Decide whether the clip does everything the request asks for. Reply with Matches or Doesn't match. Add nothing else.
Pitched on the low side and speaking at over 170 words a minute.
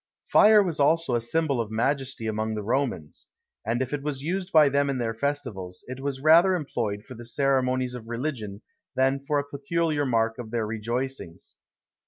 Matches